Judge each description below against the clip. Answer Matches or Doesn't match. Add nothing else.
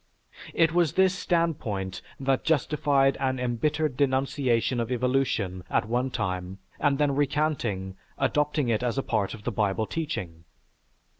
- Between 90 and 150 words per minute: Matches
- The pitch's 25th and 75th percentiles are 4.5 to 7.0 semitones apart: Matches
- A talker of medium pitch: Doesn't match